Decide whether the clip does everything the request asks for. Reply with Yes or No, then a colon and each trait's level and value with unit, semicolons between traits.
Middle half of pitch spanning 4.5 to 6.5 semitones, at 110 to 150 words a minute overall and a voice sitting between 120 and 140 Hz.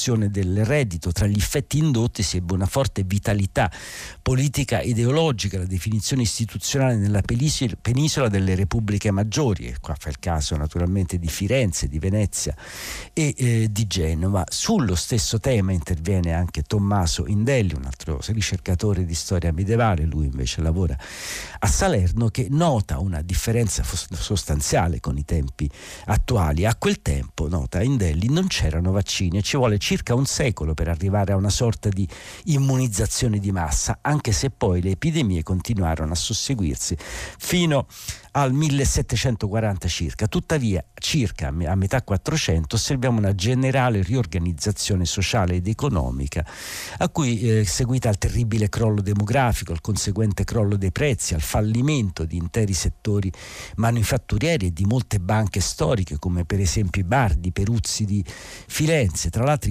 No: average, 4.8 semitones; average, 145 wpm; low, 100 Hz